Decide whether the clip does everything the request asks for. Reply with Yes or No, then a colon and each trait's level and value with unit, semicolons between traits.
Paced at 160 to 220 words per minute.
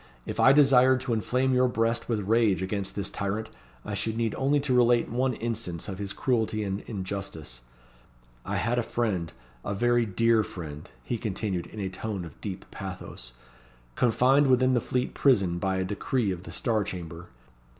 Yes: average, 180 wpm